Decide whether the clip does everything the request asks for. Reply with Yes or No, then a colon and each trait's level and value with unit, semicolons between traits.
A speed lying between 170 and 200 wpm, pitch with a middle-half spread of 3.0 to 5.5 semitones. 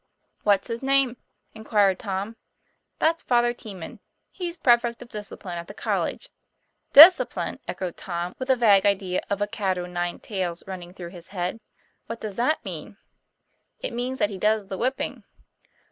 No: average, 160 wpm; average, 4.4 semitones